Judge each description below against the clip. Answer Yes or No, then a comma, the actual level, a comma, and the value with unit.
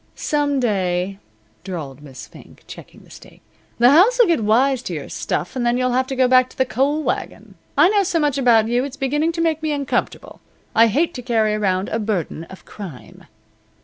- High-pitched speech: Yes, very high, 250 Hz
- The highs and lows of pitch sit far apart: Yes, wide, 5.7 semitones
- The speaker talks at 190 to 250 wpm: Yes, fast, 205 wpm